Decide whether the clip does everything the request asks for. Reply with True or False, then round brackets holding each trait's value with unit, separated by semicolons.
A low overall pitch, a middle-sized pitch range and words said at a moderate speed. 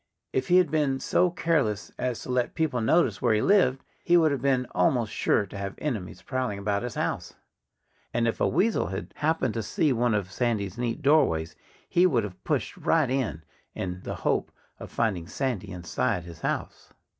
False (120 Hz; 6.4 semitones; 190 wpm)